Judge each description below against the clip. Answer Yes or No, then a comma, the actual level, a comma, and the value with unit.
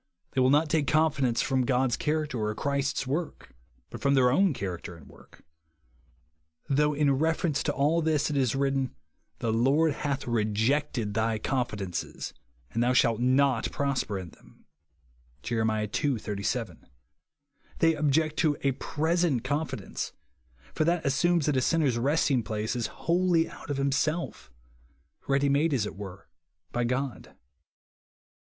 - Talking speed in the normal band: Yes, average, 150 wpm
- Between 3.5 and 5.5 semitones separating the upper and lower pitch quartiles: Yes, average, 4.4 semitones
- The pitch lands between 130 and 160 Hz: Yes, low, 135 Hz